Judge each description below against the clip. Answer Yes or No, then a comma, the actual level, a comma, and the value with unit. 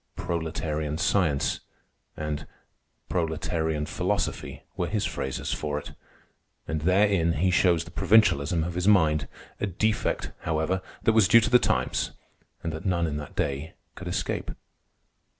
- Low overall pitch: Yes, very low, 80 Hz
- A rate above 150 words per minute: No, slow, 135 wpm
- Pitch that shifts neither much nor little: Yes, average, 3.4 semitones